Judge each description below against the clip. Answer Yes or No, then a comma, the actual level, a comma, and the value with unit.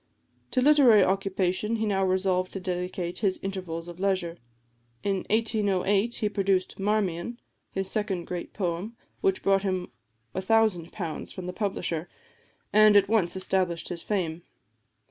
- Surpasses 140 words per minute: No, slow, 135 wpm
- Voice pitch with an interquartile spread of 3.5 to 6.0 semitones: No, average, 2.7 semitones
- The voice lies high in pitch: Yes, high, 195 Hz